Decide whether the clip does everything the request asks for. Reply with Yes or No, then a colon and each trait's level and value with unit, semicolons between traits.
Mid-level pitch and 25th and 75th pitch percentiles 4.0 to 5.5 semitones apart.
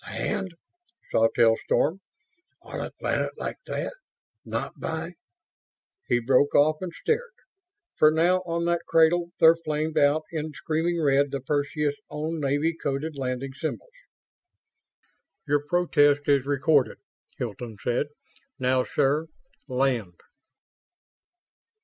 No: medium, 145 Hz; average, 3.2 semitones